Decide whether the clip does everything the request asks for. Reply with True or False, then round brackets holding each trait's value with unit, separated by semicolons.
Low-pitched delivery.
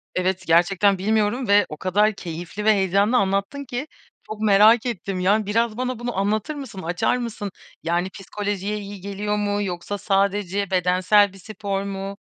False (200 Hz)